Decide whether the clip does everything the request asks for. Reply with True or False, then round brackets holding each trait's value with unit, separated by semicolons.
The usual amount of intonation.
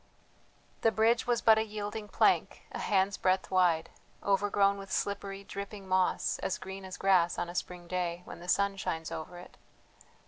False (2.1 semitones)